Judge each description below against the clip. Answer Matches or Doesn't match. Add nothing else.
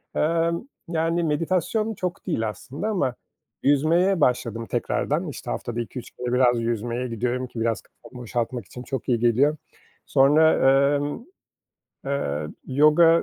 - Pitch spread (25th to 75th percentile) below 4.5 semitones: Doesn't match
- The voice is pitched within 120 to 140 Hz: Matches